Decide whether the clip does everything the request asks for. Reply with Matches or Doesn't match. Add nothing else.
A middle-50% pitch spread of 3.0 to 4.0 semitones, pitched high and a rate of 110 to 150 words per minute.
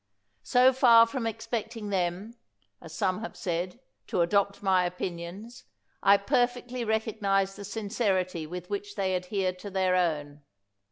Matches